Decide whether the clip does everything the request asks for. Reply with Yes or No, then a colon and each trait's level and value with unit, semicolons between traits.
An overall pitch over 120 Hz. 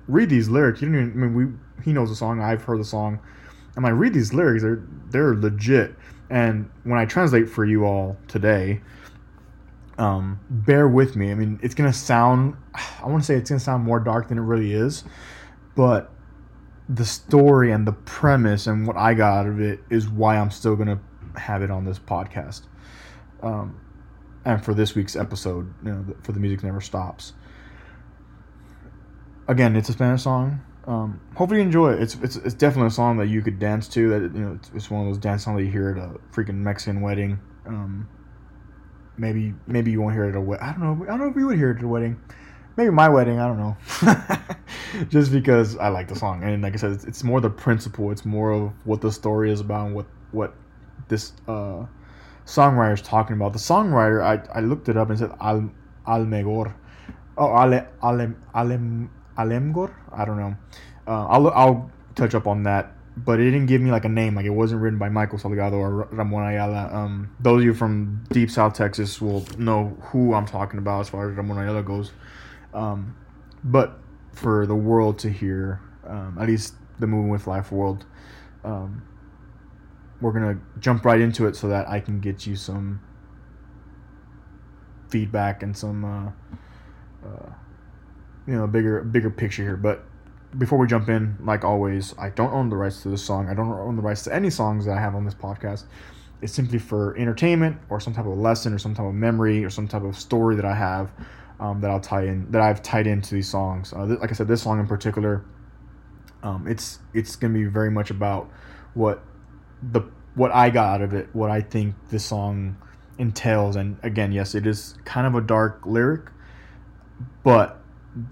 No: low, 110 Hz